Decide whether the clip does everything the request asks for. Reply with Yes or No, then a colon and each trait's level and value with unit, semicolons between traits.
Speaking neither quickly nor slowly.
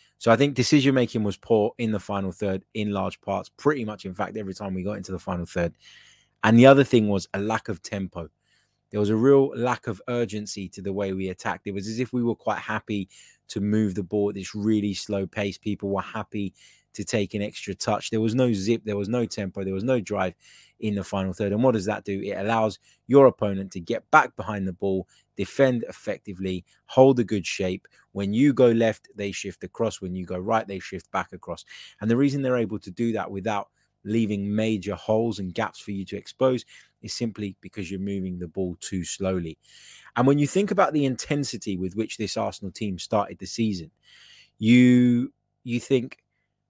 No: fast, 215 wpm